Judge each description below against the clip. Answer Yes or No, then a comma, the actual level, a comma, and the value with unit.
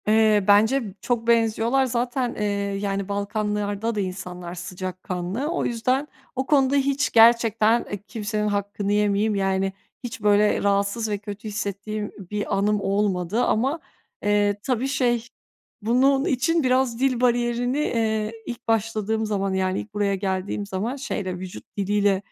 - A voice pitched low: No, high, 210 Hz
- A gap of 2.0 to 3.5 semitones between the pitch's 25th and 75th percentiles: Yes, average, 3.0 semitones